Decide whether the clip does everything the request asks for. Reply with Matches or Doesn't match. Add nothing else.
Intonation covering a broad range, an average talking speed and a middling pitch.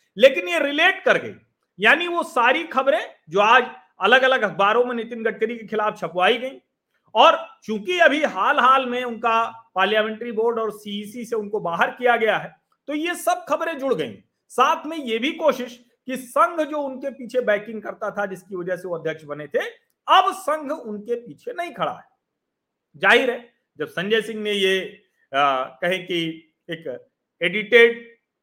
Doesn't match